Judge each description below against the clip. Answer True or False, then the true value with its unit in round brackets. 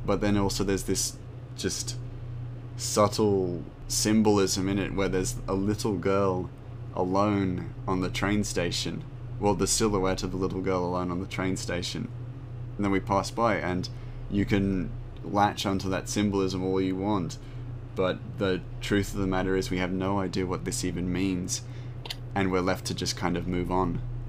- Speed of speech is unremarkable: True (175 wpm)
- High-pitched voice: False (100 Hz)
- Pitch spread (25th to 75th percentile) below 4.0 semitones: False (4.4 semitones)